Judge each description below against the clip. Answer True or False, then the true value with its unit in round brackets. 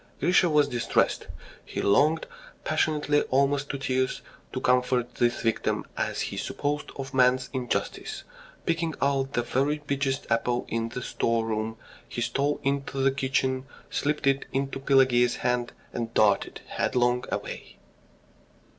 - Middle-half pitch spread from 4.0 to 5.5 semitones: False (2.4 semitones)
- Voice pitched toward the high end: False (130 Hz)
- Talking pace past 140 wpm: False (135 wpm)